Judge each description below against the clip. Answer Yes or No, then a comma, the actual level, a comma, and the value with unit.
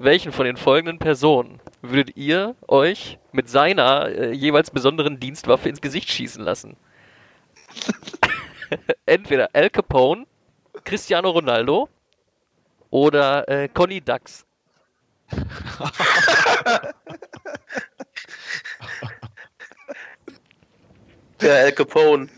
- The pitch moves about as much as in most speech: Yes, average, 4.1 semitones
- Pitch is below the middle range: No, medium, 150 Hz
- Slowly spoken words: Yes, slow, 80 wpm